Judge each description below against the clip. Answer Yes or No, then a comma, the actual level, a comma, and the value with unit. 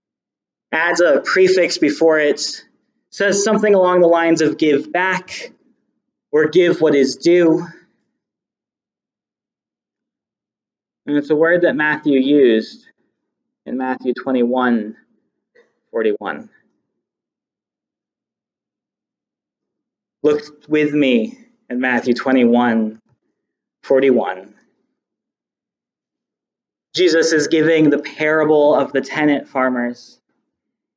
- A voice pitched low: No, medium, 150 Hz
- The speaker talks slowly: Yes, slow, 85 wpm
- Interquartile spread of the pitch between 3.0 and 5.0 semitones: Yes, average, 4.7 semitones